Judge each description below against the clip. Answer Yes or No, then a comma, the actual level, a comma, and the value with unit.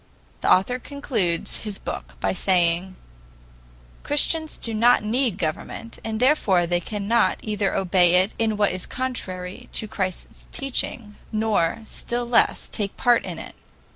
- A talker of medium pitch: No, high, 210 Hz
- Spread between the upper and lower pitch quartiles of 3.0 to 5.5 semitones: Yes, average, 4.5 semitones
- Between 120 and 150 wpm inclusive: Yes, average, 140 wpm